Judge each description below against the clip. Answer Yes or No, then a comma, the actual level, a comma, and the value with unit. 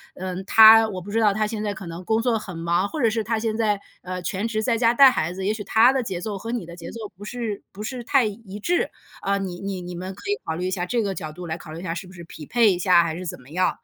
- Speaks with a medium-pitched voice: No, high, 200 Hz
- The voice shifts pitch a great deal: No, average, 3.9 semitones